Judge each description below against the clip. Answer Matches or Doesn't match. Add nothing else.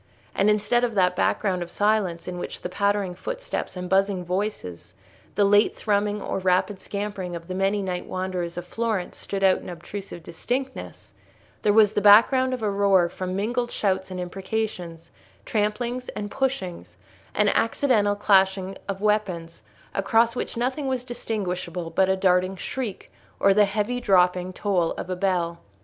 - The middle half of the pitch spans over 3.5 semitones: Doesn't match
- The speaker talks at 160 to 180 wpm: Matches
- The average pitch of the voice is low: Doesn't match